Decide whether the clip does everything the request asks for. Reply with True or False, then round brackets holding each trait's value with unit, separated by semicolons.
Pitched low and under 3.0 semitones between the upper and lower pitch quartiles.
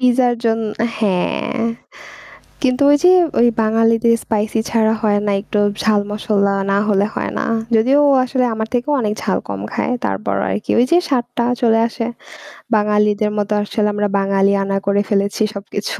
False (215 Hz; 2.6 semitones)